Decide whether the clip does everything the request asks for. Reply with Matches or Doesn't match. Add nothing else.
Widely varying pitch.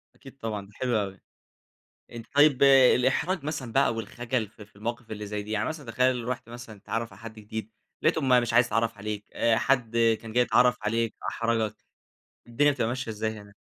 Doesn't match